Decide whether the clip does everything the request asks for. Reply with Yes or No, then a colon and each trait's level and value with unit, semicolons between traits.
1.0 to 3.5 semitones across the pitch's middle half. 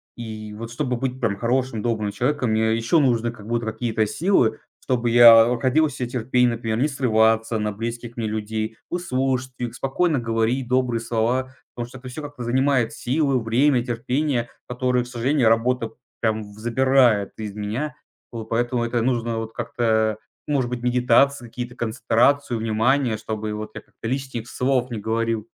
Yes: narrow, 2.4 semitones